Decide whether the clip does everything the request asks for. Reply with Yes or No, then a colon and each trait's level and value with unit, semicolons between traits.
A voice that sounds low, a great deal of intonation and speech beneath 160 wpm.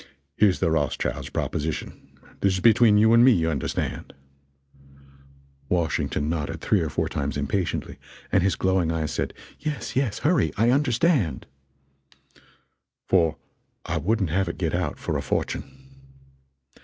Yes: very low, 95 Hz; wide, 6.0 semitones; average, 145 wpm